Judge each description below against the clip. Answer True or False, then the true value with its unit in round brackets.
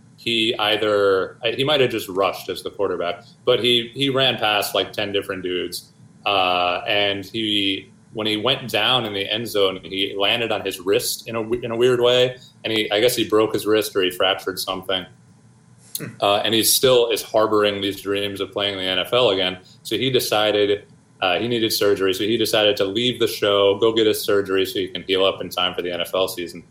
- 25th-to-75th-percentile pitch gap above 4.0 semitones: False (3.4 semitones)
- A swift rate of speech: True (215 wpm)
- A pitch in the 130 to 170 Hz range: False (105 Hz)